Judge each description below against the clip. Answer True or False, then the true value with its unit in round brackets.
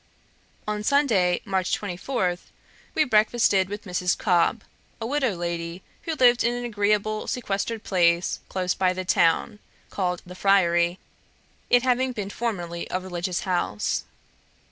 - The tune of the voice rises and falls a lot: False (4.2 semitones)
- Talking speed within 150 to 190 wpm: False (135 wpm)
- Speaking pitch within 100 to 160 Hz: False (195 Hz)